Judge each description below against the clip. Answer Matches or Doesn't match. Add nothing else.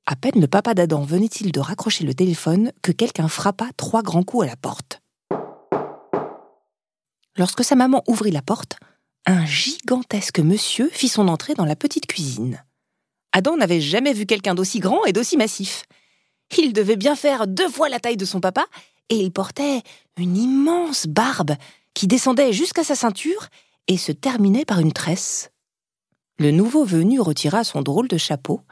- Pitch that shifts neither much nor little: Doesn't match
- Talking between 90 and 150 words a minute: Doesn't match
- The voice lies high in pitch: Matches